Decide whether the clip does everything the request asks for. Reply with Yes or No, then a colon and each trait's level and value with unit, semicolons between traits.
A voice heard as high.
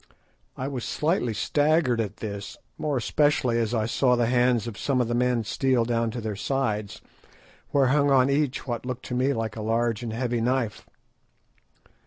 No: low, 120 Hz